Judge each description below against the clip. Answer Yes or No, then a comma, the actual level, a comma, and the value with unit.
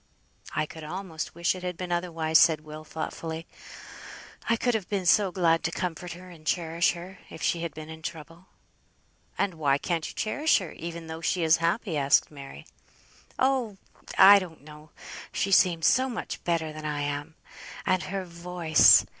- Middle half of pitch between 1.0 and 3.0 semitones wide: Yes, average, 2.7 semitones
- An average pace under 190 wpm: Yes, average, 180 wpm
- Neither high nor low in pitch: Yes, medium, 170 Hz